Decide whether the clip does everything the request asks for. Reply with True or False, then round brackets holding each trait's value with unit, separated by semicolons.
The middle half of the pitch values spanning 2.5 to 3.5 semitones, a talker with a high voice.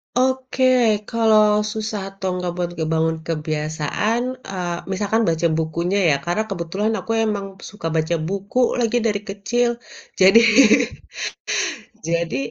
False (4.6 semitones; 195 Hz)